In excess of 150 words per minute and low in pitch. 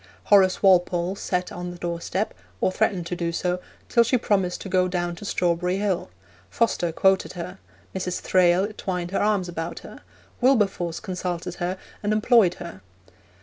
No: average, 160 wpm; medium, 180 Hz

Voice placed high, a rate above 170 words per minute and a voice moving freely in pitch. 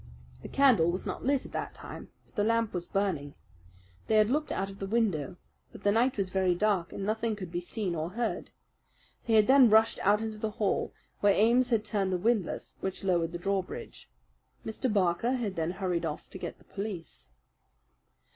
No: high, 205 Hz; average, 200 wpm; average, 3.6 semitones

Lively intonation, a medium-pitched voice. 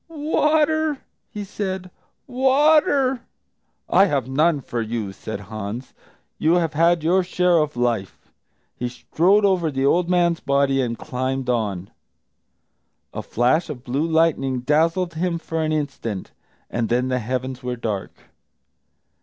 Yes: wide, 6.5 semitones; medium, 150 Hz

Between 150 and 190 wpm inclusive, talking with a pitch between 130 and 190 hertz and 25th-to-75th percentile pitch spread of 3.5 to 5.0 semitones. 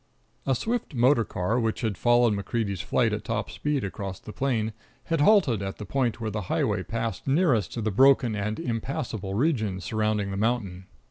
No: average, 185 wpm; low, 115 Hz; average, 4.2 semitones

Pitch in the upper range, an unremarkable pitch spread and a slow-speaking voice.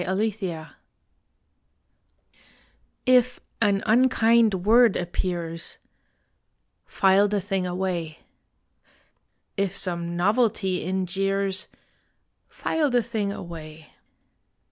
Yes: high, 195 Hz; average, 3.7 semitones; slow, 80 wpm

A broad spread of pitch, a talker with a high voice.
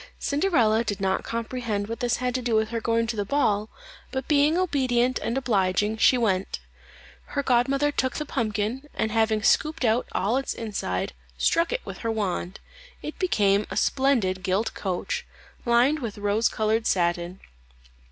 No: average, 4.2 semitones; high, 230 Hz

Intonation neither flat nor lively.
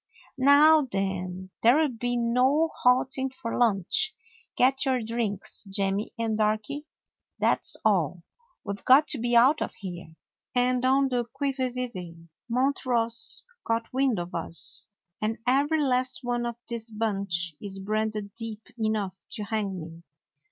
Yes: average, 4.3 semitones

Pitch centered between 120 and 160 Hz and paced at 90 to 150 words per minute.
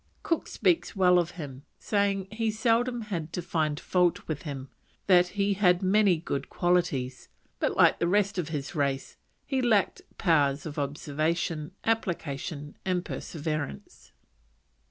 No: medium, 175 Hz; average, 140 wpm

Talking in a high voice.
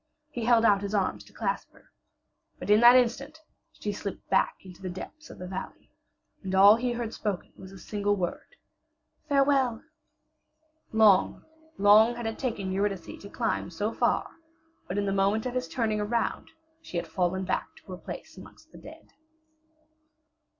Yes: high, 205 Hz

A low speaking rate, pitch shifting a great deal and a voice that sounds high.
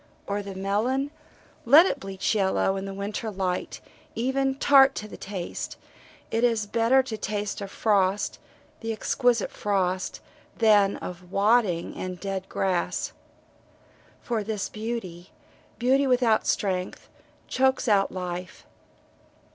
No: slow, 130 wpm; average, 3.7 semitones; high, 205 Hz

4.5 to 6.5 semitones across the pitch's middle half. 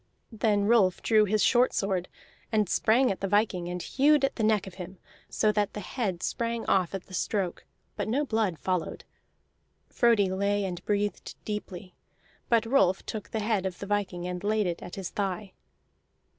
No: average, 2.9 semitones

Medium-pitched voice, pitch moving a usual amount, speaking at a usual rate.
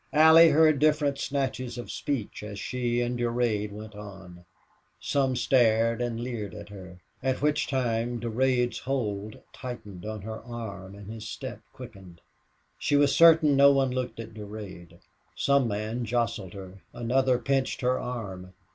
No: low, 120 Hz; average, 4.1 semitones; average, 150 wpm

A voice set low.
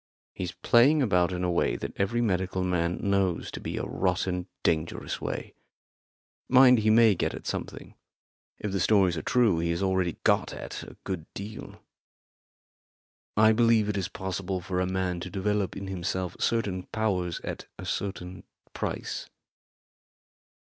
Yes: very low, 95 Hz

